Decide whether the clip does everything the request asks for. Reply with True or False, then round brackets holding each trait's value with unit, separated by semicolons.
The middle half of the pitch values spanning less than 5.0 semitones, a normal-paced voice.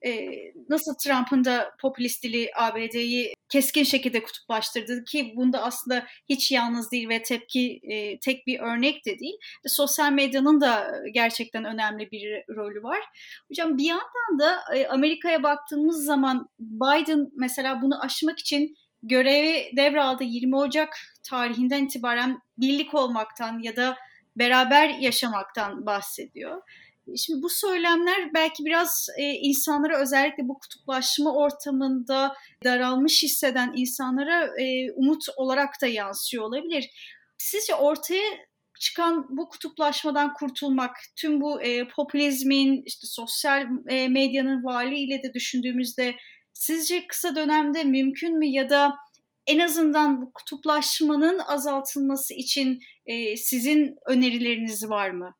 True (3.2 semitones; 115 wpm)